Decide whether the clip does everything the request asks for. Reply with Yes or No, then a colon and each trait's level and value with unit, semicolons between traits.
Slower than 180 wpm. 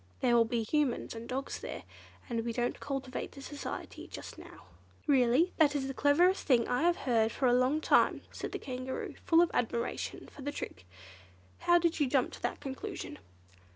No: average, 190 wpm